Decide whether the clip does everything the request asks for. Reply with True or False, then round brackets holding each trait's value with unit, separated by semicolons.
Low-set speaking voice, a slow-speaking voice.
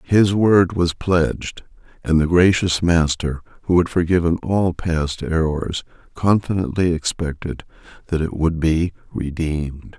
True (85 Hz; 125 wpm)